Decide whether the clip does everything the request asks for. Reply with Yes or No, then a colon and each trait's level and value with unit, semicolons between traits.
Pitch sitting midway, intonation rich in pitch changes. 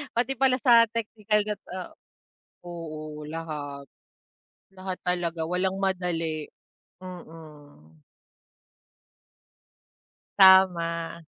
No: medium, 175 Hz; average, 3.2 semitones